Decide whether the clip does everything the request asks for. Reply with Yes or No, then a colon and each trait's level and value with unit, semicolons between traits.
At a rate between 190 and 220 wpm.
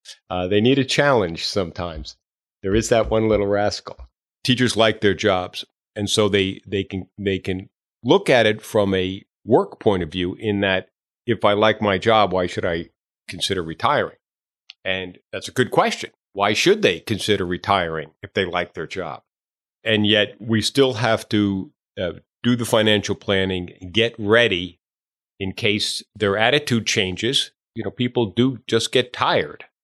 No: average, 170 wpm